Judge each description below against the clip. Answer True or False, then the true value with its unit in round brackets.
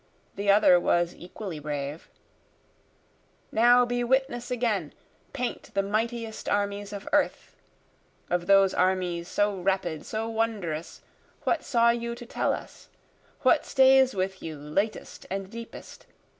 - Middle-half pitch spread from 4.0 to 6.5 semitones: True (4.7 semitones)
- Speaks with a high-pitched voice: True (205 Hz)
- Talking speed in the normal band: False (130 wpm)